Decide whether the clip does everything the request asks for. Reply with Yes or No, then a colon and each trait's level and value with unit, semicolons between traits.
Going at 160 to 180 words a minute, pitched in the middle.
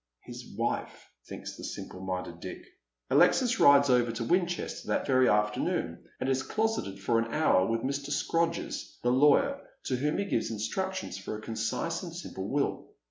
No: average, 175 wpm; low, 130 Hz